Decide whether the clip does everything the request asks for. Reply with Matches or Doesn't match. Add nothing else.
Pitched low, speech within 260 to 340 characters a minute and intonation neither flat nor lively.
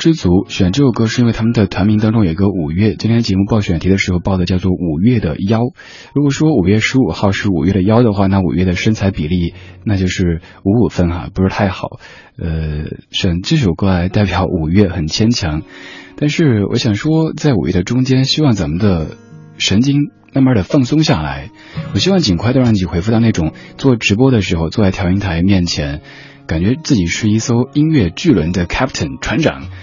Matches